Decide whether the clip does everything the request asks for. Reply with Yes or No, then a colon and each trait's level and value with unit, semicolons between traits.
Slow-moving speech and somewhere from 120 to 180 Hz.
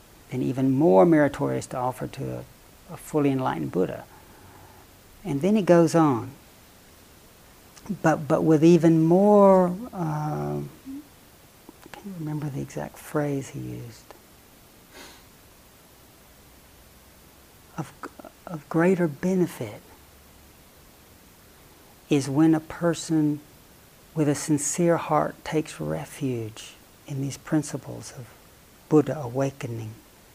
Yes: slow, 100 wpm; medium, 140 Hz